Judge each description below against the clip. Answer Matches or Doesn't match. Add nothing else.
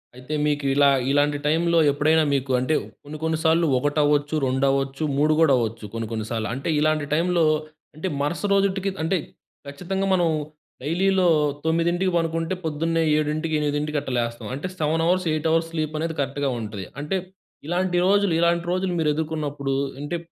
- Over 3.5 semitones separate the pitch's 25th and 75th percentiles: Doesn't match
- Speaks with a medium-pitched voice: Matches